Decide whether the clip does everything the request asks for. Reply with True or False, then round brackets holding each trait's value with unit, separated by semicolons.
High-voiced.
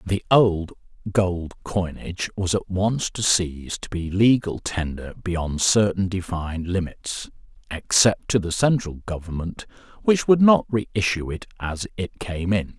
False (95 Hz)